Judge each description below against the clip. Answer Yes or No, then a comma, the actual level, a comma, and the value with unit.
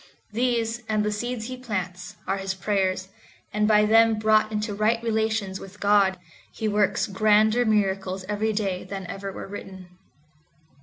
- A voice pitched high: Yes, high, 210 Hz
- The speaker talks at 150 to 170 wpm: Yes, average, 155 wpm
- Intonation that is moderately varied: No, narrow, 2.2 semitones